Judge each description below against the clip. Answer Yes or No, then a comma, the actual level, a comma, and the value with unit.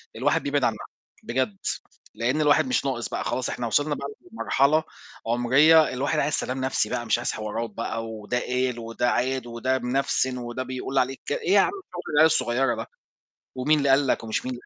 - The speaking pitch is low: Yes, low, 130 Hz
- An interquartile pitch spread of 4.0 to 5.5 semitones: No, average, 2.9 semitones